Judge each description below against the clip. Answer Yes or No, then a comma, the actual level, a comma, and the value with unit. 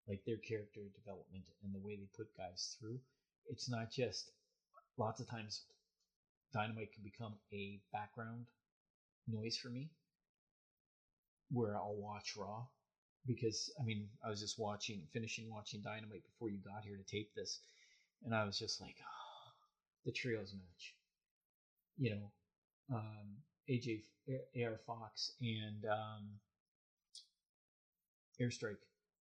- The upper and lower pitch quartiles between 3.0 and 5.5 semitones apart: No, narrow, 2.6 semitones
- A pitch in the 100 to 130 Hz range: Yes, low, 110 Hz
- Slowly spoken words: Yes, slow, 130 wpm